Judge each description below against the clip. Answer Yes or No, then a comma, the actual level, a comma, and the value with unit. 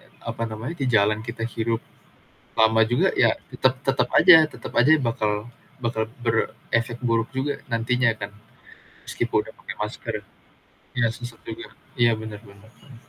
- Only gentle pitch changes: Yes, narrow, 1.8 semitones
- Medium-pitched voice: No, low, 115 Hz